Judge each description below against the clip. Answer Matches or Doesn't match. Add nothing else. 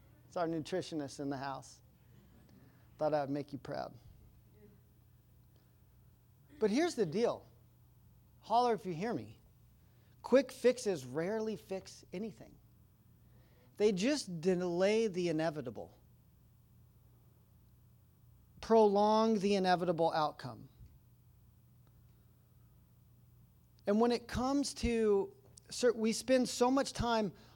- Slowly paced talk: Matches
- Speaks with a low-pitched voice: Doesn't match